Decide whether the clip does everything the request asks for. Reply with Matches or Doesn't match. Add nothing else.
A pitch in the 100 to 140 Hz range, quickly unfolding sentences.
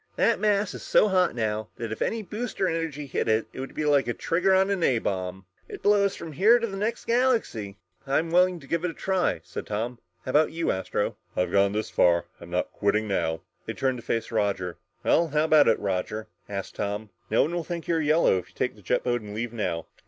Matches